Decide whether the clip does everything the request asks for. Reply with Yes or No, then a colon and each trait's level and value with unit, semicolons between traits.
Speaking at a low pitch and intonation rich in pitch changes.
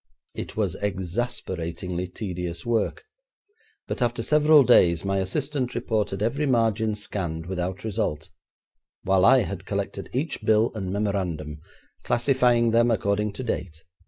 No: low, 105 Hz; average, 4.5 semitones